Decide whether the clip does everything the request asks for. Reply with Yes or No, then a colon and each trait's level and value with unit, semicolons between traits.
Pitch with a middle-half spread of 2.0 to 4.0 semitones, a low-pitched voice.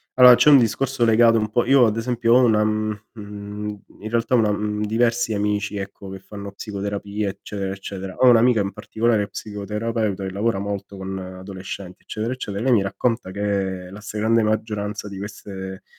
Yes: narrow, 2.5 semitones; low, 105 Hz